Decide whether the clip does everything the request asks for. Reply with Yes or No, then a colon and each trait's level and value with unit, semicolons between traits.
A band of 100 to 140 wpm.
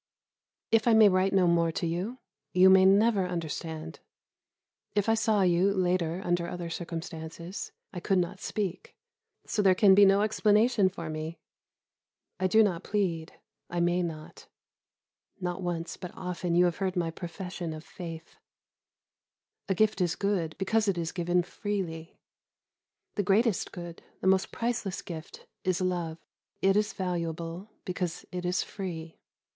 No: average, 150 wpm